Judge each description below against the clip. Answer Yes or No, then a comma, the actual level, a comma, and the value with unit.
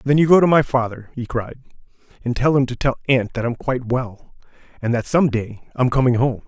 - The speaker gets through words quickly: Yes, fast, 230 wpm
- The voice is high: No, low, 125 Hz